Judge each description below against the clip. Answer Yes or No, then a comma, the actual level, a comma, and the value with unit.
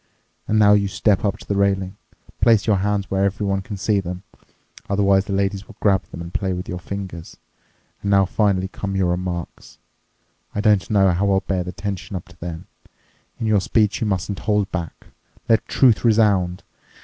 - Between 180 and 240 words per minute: Yes, average, 190 wpm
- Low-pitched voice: Yes, low, 100 Hz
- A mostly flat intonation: Yes, narrow, 1.8 semitones